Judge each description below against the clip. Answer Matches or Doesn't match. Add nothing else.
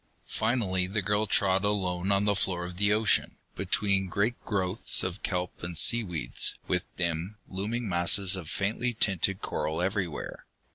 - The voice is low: Matches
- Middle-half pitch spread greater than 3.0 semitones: Doesn't match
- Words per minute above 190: Doesn't match